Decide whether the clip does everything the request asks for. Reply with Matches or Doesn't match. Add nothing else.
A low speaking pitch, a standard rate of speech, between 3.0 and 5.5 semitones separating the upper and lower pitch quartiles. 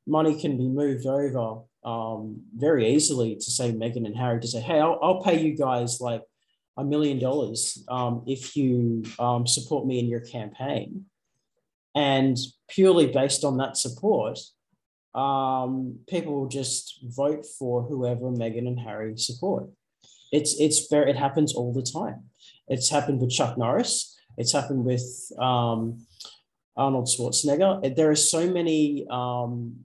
Matches